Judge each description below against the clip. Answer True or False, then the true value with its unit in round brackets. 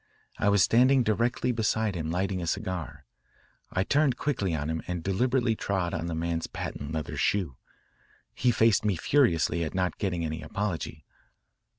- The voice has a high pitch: False (95 Hz)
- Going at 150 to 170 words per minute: True (165 wpm)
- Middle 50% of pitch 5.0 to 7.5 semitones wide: True (5.4 semitones)